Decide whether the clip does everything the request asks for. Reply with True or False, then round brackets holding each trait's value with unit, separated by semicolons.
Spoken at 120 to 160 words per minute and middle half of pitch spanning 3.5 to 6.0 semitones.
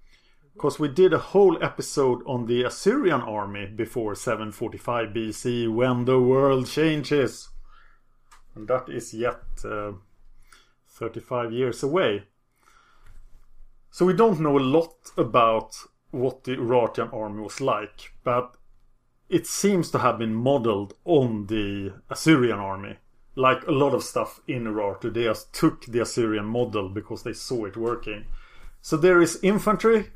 True (140 wpm; 4.3 semitones)